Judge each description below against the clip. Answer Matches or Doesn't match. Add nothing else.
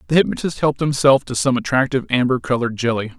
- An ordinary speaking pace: Matches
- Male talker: Matches